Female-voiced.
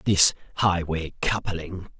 No: male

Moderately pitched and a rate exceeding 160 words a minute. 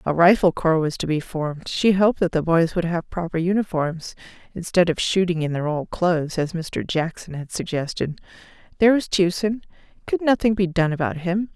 Yes: medium, 175 Hz; average, 190 wpm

